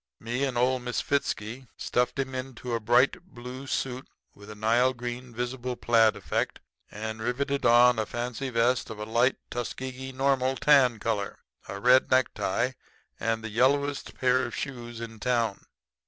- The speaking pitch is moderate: No, low, 125 Hz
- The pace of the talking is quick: No, average, 155 wpm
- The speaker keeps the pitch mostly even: Yes, narrow, 2.2 semitones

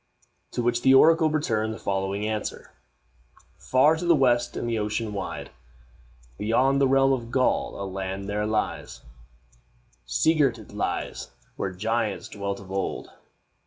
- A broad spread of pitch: No, average, 4.9 semitones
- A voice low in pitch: Yes, low, 110 Hz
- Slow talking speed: No, average, 150 wpm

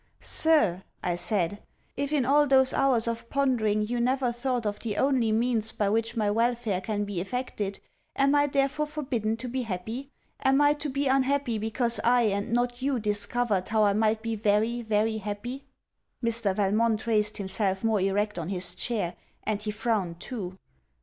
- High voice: Yes, high, 225 Hz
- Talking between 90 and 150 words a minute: No, average, 175 wpm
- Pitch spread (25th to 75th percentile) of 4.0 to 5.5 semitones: No, average, 3.5 semitones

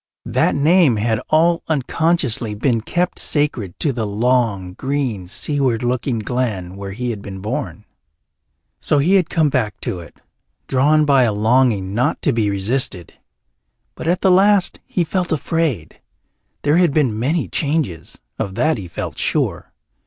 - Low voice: Yes, low, 125 Hz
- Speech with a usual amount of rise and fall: No, wide, 6.7 semitones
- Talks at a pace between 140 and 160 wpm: Yes, average, 155 wpm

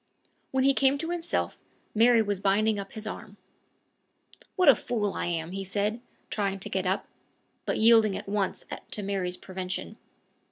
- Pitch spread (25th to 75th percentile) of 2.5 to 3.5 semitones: Yes, average, 3.0 semitones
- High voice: Yes, high, 205 Hz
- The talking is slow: No, average, 165 wpm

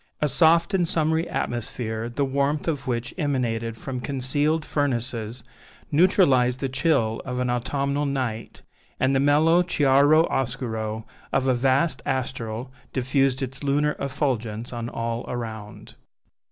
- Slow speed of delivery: Yes, slow, 130 wpm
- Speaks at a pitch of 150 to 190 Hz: No, low, 130 Hz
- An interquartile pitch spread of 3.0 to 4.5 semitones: Yes, average, 3.3 semitones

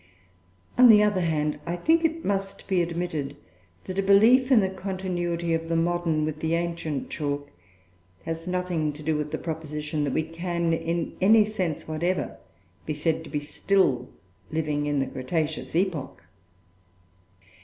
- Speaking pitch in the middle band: Yes, medium, 165 Hz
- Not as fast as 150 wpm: No, average, 160 wpm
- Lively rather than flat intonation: No, average, 3.4 semitones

